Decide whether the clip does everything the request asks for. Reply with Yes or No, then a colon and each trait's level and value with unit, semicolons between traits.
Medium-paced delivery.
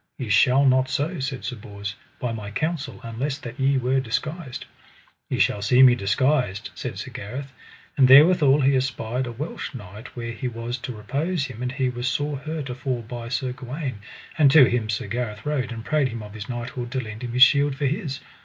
No: fast, 210 wpm